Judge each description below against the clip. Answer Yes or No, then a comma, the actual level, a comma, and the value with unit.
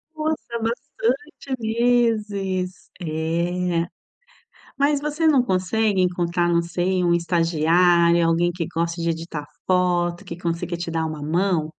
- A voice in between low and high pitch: Yes, medium, 175 Hz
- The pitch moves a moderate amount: Yes, average, 3.7 semitones